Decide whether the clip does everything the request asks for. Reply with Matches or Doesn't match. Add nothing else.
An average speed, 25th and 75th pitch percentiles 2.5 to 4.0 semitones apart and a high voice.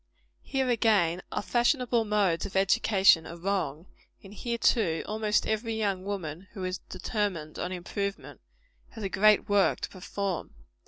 Matches